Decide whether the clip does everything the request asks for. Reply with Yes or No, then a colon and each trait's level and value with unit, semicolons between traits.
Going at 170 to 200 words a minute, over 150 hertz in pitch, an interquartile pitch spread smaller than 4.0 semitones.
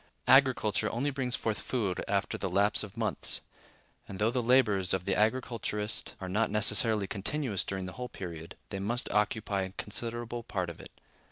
No: average, 175 wpm; low, 105 Hz; average, 3.6 semitones